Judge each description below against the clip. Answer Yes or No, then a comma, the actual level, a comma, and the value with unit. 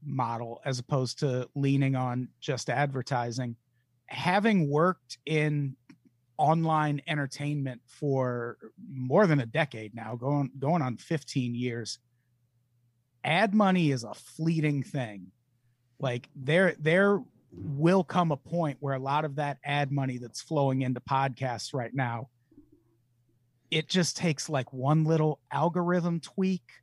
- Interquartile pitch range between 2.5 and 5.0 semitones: Yes, average, 4.2 semitones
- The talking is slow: Yes, slow, 130 wpm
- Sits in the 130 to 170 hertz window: Yes, medium, 140 Hz